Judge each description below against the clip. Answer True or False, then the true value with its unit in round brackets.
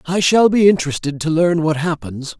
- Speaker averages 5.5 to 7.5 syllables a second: False (5.3 syllables/s)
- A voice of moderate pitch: True (165 Hz)